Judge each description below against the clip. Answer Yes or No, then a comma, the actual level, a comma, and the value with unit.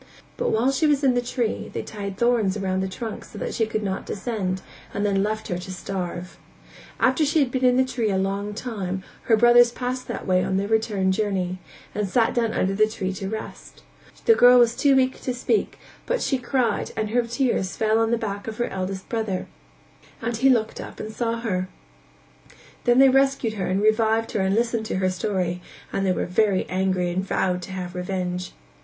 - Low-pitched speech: No, high, 215 Hz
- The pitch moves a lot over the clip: No, average, 4.1 semitones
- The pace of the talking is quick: Yes, fast, 210 wpm